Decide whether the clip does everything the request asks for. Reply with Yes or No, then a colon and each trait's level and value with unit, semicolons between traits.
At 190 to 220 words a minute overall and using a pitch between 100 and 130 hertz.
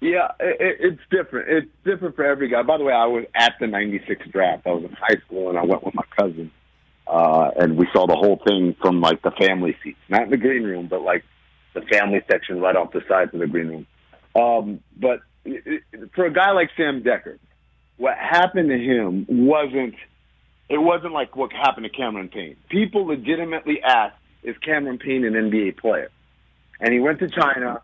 Yes: fast, 205 wpm; low, 125 Hz